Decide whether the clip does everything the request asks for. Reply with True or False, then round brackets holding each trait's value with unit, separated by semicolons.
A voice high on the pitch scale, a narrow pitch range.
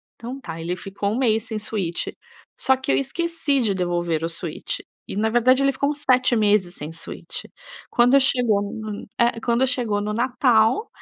False (225 Hz; 4.3 semitones)